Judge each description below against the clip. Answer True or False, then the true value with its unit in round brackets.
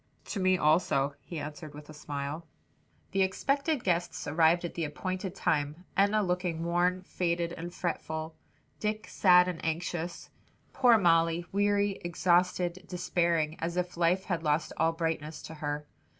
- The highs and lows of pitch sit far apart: False (2.4 semitones)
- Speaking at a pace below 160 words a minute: True (150 wpm)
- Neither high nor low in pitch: True (175 Hz)